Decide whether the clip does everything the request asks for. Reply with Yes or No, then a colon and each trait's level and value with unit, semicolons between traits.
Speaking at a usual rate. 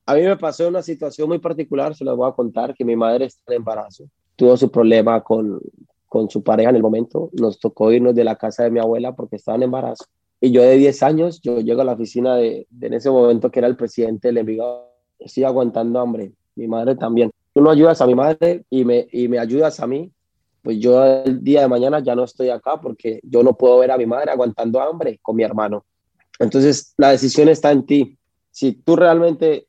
No: fast, 230 wpm